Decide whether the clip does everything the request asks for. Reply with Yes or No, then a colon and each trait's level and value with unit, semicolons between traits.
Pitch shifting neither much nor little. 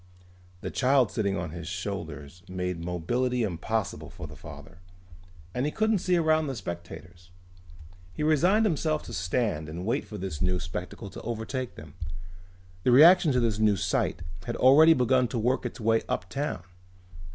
No: wide, 7.0 semitones